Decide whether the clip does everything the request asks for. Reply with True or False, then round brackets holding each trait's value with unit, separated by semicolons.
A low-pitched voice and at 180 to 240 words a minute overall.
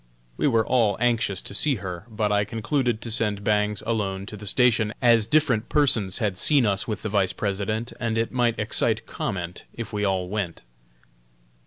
True (110 Hz; 185 wpm)